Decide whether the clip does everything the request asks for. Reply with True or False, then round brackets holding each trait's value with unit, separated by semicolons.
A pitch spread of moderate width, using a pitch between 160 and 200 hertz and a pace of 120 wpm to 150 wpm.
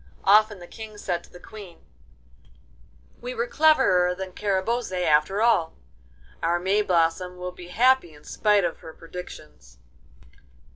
True (3.5 semitones; 185 Hz; 135 wpm)